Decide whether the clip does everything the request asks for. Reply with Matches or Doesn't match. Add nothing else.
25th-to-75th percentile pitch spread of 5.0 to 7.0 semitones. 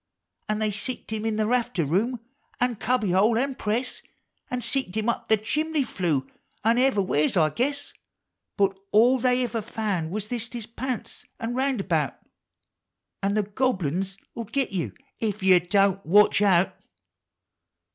Doesn't match